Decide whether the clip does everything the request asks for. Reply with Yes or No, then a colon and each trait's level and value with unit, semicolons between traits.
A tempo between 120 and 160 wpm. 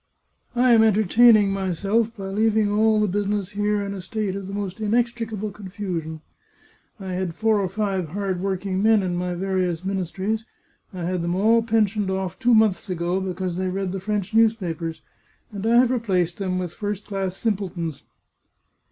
No: average, 180 wpm